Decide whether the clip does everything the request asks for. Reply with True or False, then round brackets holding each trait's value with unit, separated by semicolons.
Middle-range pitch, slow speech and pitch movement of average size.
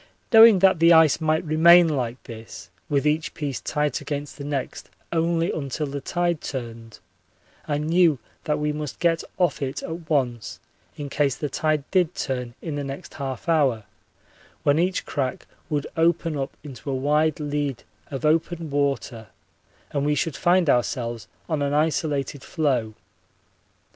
False (150 Hz; 160 wpm; 3.0 semitones)